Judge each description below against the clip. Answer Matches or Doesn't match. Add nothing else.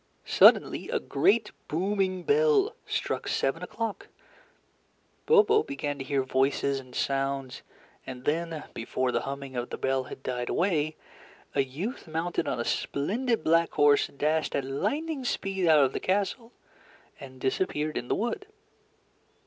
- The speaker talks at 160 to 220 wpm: Doesn't match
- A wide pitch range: Matches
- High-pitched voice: Doesn't match